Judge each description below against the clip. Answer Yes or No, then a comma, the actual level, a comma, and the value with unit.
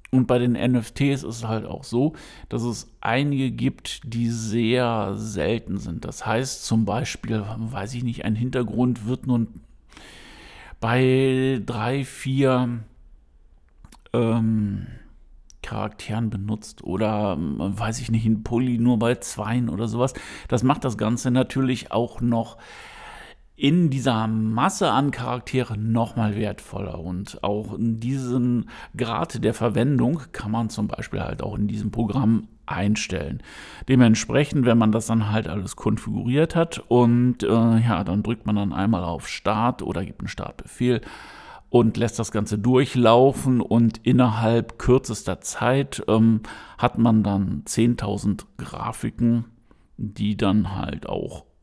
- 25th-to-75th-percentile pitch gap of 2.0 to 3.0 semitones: Yes, average, 2.7 semitones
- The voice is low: Yes, low, 115 Hz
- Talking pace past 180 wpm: No, average, 135 wpm